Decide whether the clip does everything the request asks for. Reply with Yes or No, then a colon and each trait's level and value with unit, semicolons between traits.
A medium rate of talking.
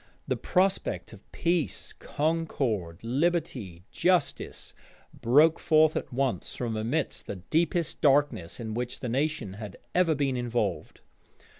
No: slow, 125 wpm